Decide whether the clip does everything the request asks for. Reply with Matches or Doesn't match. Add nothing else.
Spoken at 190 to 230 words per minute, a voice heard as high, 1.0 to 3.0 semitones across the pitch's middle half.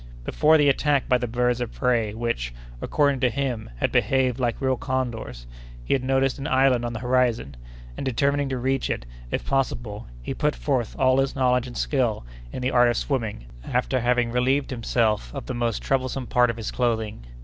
Doesn't match